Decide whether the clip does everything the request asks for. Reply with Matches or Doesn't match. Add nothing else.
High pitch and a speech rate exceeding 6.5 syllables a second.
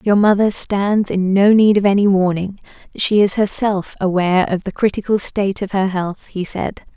Doesn't match